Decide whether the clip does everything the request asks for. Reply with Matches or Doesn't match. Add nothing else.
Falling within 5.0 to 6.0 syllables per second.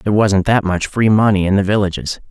Matches